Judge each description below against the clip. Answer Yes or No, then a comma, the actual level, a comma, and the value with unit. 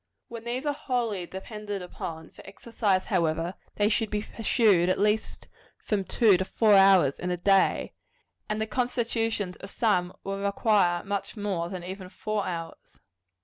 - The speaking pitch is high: Yes, high, 200 Hz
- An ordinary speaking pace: Yes, average, 160 wpm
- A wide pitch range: No, average, 3.2 semitones